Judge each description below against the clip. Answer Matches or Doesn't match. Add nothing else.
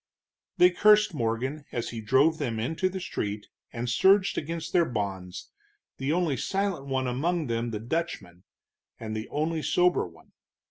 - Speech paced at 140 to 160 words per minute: Matches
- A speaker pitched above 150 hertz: Doesn't match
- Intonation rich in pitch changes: Matches